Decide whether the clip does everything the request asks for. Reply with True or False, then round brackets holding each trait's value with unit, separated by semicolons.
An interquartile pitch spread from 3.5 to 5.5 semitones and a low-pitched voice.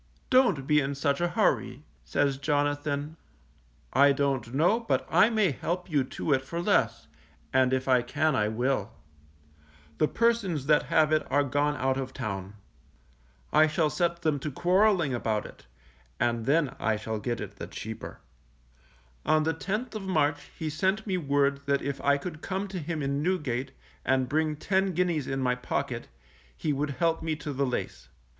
False (4.2 semitones; 145 Hz)